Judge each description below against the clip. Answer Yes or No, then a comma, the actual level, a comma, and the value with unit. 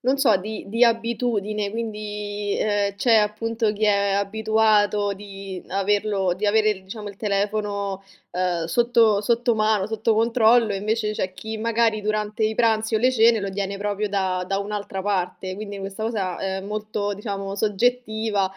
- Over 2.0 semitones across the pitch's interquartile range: No, narrow, 1.7 semitones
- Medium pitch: No, high, 210 Hz